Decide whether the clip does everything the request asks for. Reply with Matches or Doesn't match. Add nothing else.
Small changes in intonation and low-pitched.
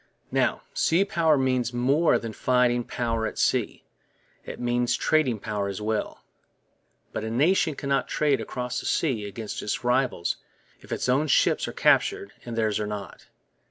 Doesn't match